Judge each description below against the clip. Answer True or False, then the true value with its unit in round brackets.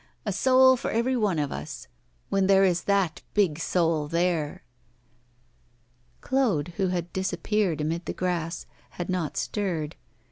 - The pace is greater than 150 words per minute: False (140 wpm)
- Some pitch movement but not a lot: True (3.7 semitones)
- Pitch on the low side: False (180 Hz)